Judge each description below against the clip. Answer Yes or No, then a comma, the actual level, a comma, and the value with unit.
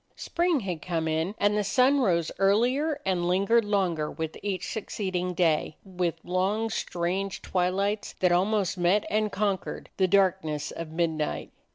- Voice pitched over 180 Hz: Yes, high, 190 Hz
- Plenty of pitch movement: No, average, 3.1 semitones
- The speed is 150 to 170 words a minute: Yes, average, 155 wpm